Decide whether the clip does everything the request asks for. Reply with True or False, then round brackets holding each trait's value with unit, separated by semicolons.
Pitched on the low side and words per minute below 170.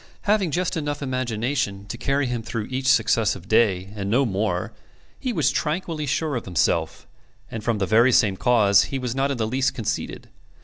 False (120 Hz; 185 wpm)